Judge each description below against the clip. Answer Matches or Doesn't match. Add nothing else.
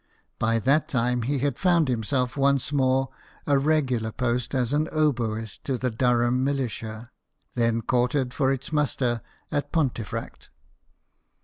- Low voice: Matches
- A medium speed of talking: Doesn't match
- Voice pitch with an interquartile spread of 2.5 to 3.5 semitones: Matches